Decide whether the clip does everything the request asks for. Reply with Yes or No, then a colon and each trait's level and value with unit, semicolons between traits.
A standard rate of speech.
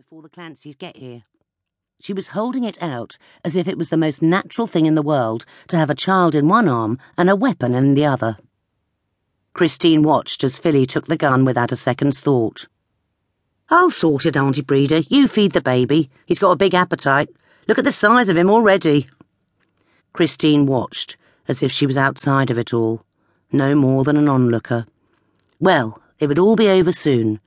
Yes: average, 190 wpm